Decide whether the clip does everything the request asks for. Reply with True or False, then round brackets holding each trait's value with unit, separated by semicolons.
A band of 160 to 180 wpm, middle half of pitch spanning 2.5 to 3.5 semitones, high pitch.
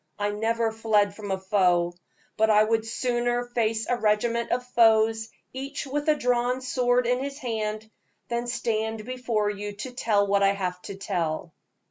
True (170 wpm; 2.8 semitones; 225 Hz)